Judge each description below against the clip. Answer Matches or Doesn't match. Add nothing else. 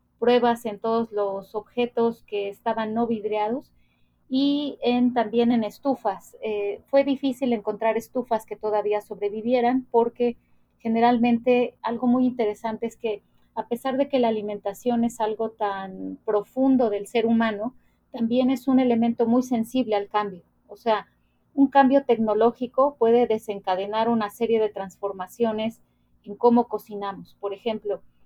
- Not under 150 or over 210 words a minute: Doesn't match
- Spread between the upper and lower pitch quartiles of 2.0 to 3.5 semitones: Matches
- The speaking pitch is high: Matches